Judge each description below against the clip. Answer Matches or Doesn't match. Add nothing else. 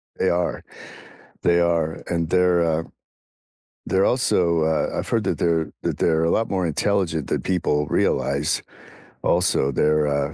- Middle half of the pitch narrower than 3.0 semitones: Matches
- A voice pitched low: Matches